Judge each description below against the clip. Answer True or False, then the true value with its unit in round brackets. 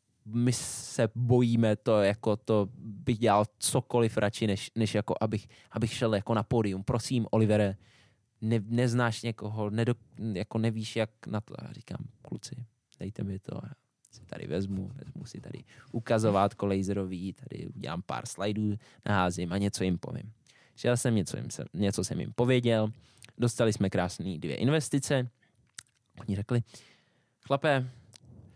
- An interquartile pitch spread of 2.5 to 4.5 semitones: True (2.8 semitones)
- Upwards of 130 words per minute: True (145 wpm)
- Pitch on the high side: False (115 Hz)